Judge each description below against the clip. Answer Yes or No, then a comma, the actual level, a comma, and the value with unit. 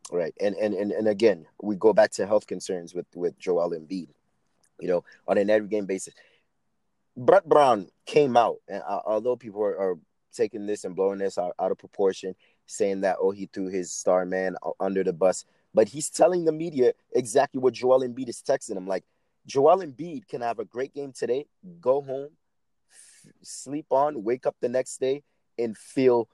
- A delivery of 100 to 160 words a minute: No, average, 195 wpm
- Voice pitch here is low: Yes, low, 130 Hz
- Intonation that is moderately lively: No, wide, 8.5 semitones